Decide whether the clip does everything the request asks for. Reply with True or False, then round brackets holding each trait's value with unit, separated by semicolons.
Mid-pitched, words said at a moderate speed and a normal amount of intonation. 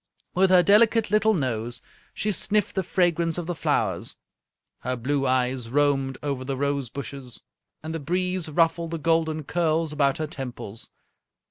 True (155 Hz; 155 wpm; 4.7 semitones)